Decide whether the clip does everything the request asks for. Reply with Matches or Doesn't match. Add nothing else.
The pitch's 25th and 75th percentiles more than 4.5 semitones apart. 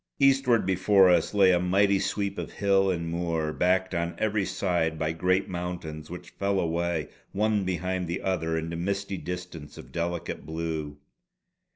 Doesn't match